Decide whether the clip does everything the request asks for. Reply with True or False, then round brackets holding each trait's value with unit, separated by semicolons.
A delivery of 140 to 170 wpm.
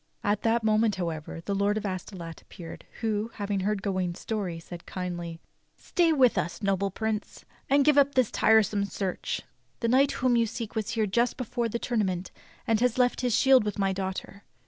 False (190 wpm)